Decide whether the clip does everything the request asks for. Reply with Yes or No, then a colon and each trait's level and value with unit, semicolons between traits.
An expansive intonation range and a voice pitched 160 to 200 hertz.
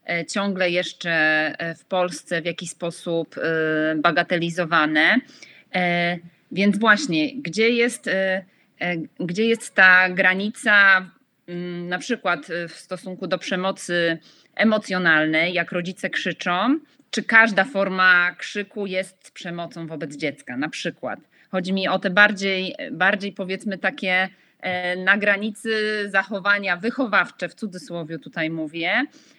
No: average, 2.9 semitones; medium, 185 Hz